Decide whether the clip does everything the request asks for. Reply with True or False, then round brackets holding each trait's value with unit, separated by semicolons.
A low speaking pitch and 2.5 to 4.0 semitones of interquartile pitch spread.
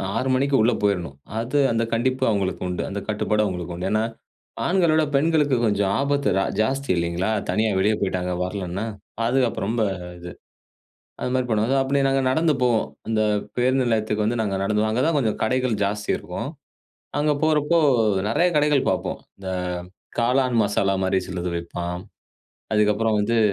False (110 Hz; 5.0 semitones)